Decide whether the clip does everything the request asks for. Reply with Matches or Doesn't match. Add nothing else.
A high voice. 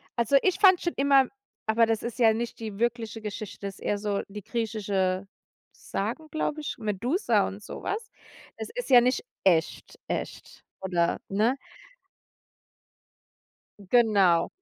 Matches